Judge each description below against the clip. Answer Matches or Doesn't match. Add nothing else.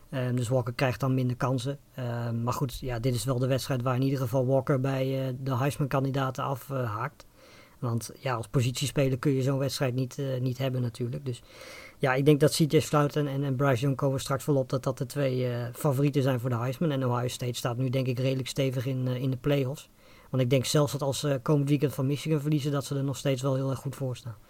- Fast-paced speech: Matches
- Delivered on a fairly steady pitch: Matches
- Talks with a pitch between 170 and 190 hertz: Doesn't match